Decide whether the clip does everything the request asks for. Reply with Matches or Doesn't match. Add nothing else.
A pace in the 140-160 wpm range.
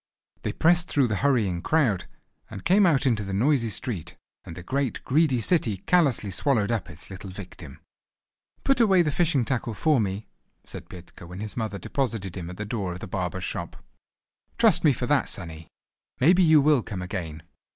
Doesn't match